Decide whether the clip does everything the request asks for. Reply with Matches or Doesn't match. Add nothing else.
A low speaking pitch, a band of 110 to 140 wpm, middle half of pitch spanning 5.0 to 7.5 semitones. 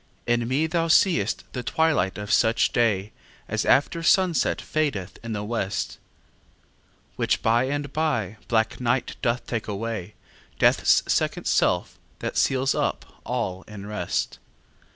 Matches